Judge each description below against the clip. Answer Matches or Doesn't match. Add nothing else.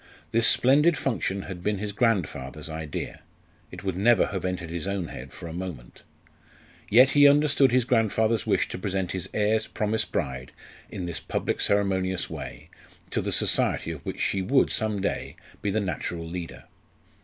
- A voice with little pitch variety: Doesn't match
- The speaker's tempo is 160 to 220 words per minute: Matches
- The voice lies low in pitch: Matches